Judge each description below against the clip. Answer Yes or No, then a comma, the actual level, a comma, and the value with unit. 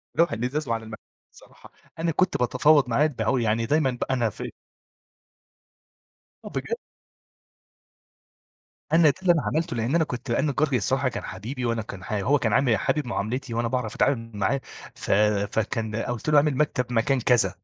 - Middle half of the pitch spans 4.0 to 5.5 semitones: Yes, average, 4.3 semitones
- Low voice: Yes, low, 125 Hz